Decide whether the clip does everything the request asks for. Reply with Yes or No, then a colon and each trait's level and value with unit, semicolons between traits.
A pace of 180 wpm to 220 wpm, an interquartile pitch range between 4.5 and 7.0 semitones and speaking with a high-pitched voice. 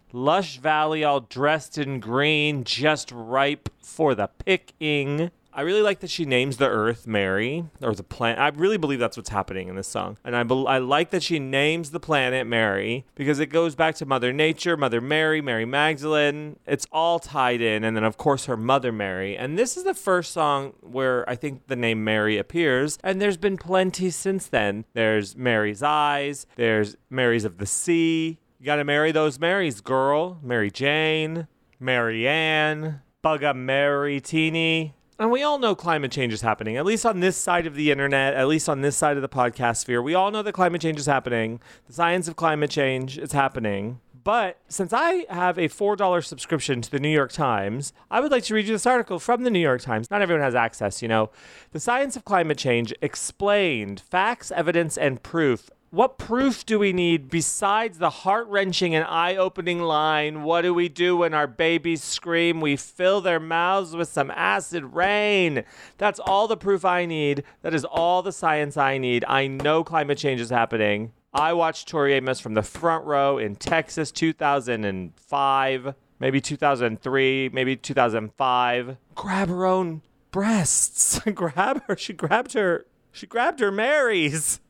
No: average, 185 wpm; average, 5.2 semitones; medium, 150 Hz